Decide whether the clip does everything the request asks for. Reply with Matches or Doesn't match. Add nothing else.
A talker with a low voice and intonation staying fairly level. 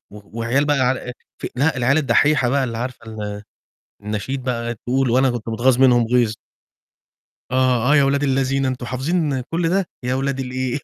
Matches